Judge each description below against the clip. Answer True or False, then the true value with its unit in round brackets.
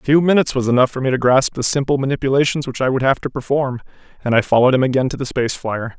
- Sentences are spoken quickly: True (270 wpm)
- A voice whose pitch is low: True (130 Hz)